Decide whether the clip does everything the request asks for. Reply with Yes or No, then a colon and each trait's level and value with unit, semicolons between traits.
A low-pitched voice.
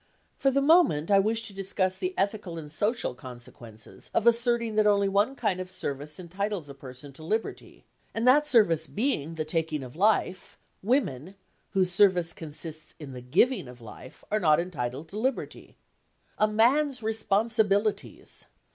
No: high, 195 Hz